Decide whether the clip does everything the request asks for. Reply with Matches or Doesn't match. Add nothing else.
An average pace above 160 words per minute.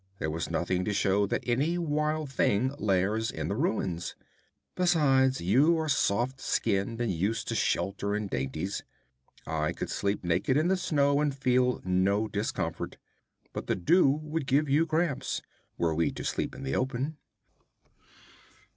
Doesn't match